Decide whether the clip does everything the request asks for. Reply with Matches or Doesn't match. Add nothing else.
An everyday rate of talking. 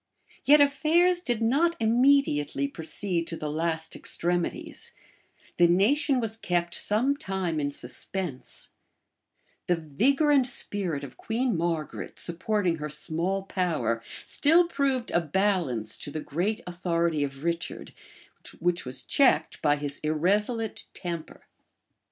Doesn't match